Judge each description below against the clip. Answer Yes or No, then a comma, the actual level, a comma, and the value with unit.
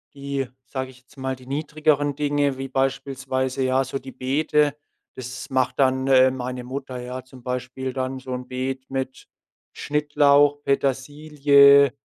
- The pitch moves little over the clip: Yes, narrow, 1.5 semitones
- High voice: No, low, 135 Hz